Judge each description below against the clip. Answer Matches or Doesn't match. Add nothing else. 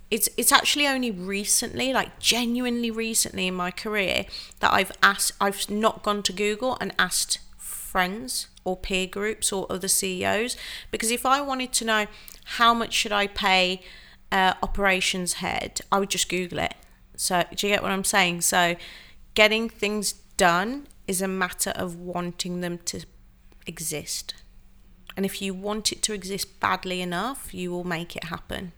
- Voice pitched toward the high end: Matches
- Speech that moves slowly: Doesn't match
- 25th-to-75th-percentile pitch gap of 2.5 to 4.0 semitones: Matches